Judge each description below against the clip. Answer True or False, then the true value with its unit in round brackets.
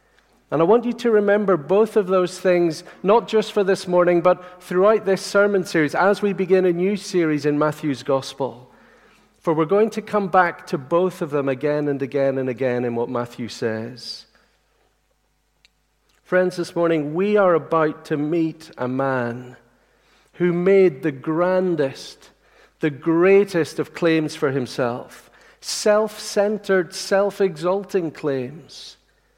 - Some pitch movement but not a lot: True (4.7 semitones)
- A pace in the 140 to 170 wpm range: True (150 wpm)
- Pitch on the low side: False (175 Hz)